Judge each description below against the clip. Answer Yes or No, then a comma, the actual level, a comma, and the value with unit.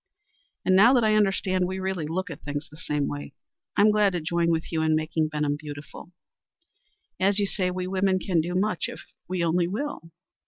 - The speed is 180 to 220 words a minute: Yes, average, 200 wpm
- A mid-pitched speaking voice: Yes, medium, 180 Hz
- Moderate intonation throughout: Yes, average, 3.4 semitones